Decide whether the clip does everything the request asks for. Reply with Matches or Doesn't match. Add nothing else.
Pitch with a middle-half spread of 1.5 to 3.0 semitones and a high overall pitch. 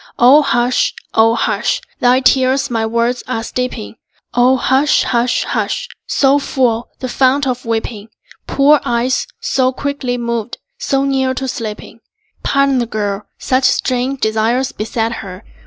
Matches